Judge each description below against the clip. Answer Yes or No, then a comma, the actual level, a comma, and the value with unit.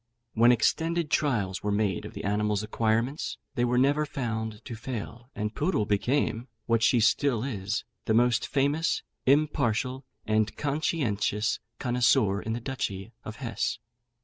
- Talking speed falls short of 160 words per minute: Yes, average, 145 wpm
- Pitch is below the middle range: Yes, low, 115 Hz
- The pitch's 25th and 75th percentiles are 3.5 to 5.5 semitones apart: Yes, average, 3.9 semitones